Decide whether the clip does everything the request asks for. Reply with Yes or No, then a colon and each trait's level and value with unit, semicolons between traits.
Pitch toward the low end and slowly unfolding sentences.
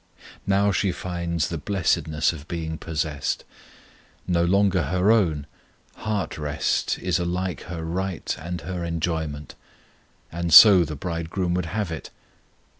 Yes: very low, 85 Hz; slow, 130 wpm